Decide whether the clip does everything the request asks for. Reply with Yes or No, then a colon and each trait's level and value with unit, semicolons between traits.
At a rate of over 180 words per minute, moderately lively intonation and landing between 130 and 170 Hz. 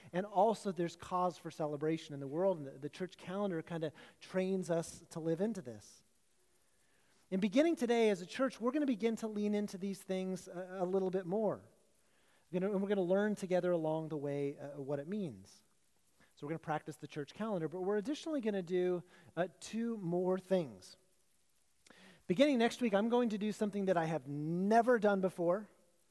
No: fast, 205 wpm; average, 4.0 semitones; medium, 185 Hz